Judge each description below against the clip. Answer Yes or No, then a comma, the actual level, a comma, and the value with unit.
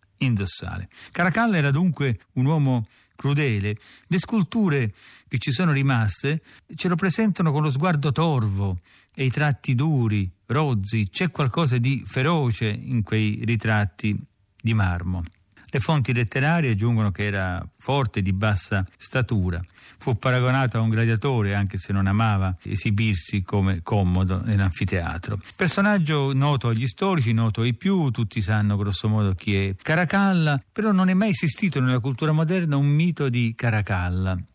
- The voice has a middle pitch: No, low, 120 Hz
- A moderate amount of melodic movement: No, wide, 6.4 semitones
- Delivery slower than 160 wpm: Yes, average, 145 wpm